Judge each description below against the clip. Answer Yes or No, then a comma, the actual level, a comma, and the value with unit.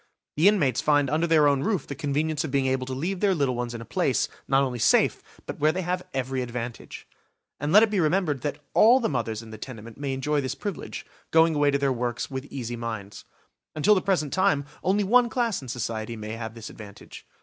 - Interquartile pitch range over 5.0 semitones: Yes, wide, 5.4 semitones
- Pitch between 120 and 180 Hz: Yes, medium, 140 Hz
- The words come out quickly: Yes, fast, 225 wpm